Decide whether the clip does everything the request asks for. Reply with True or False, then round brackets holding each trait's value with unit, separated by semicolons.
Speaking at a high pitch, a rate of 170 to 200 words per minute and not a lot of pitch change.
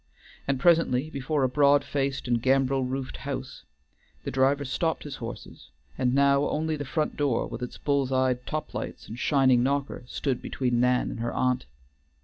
False (135 Hz; 175 wpm; 2.1 semitones)